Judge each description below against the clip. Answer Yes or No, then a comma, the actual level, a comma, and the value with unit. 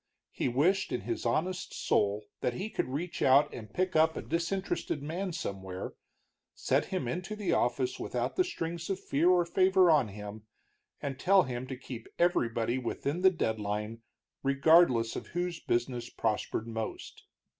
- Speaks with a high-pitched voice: No, medium, 140 Hz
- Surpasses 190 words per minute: No, average, 160 wpm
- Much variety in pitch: Yes, wide, 7.3 semitones